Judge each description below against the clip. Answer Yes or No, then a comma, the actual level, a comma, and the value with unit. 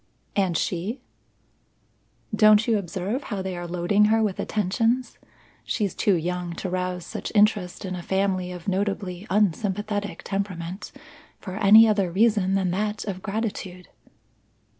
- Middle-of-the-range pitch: No, high, 195 Hz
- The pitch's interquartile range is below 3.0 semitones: Yes, narrow, 2.6 semitones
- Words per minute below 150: Yes, average, 140 wpm